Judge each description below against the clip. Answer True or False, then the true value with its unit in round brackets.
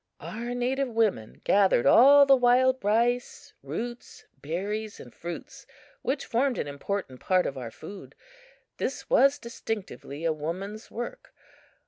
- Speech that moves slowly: True (130 wpm)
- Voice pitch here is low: False (220 Hz)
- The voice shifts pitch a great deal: True (5.9 semitones)